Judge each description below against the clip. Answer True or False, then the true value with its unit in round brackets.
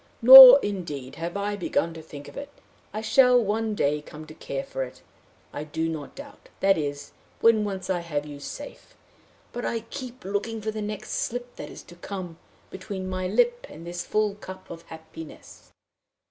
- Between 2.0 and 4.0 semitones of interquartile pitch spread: False (5.6 semitones)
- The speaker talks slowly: False (190 wpm)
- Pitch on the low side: False (190 Hz)